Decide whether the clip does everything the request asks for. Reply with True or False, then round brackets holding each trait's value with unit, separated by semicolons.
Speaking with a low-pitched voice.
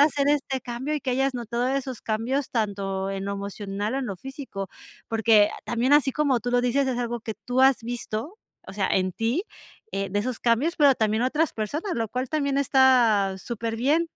False (245 Hz)